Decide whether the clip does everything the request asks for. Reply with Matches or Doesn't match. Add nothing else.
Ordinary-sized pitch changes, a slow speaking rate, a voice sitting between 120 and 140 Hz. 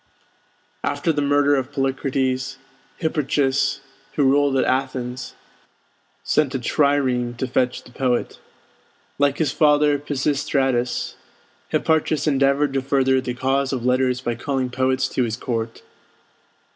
Doesn't match